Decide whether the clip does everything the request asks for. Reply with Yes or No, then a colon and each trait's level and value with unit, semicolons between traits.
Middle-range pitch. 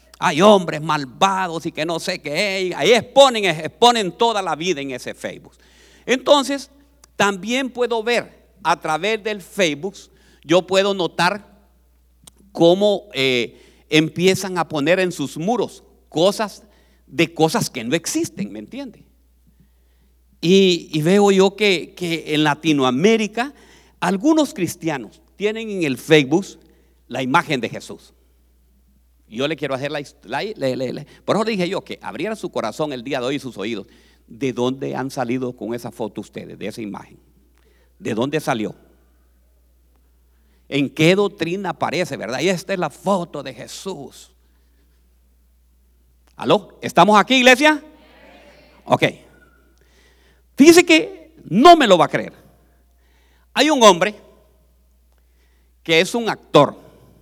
Yes: medium, 165 Hz